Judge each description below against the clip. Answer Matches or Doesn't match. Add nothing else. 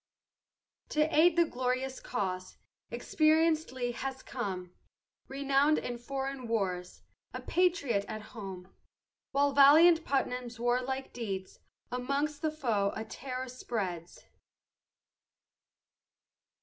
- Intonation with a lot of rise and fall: Doesn't match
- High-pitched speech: Matches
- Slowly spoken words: Matches